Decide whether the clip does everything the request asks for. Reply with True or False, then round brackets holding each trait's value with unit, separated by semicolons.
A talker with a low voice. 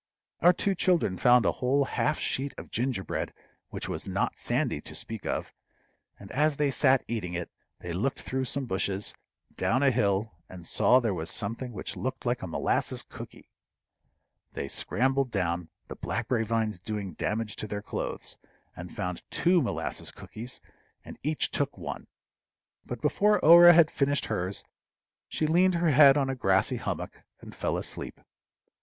True (125 Hz)